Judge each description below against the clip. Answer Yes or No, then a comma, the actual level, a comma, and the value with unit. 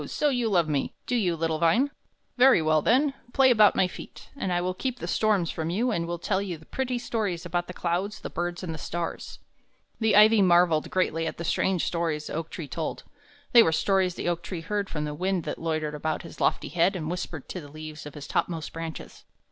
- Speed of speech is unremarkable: No, fast, 230 wpm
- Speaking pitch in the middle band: Yes, medium, 175 Hz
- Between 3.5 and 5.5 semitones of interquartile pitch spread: Yes, average, 4.1 semitones